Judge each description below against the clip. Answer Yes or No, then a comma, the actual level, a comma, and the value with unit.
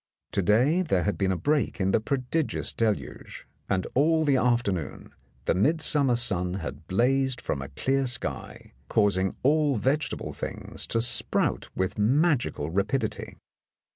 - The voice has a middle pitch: No, low, 120 Hz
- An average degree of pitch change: No, wide, 6.4 semitones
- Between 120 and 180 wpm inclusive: Yes, average, 140 wpm